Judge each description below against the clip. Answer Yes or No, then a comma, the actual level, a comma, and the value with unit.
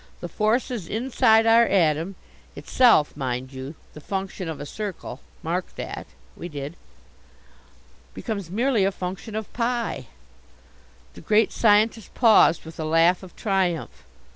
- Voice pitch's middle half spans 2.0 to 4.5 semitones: No, wide, 5.4 semitones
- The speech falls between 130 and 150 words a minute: Yes, average, 140 wpm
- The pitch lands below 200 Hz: Yes, high, 190 Hz